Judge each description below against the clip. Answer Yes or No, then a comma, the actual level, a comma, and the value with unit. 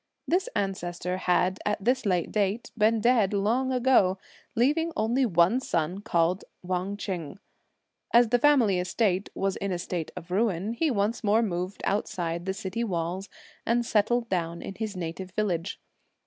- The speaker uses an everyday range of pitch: Yes, average, 4.2 semitones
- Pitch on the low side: No, high, 200 Hz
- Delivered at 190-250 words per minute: No, average, 155 wpm